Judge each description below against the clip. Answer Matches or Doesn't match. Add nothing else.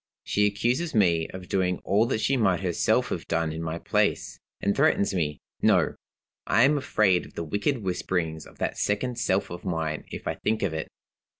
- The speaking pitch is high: Doesn't match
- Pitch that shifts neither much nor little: Matches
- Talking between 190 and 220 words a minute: Matches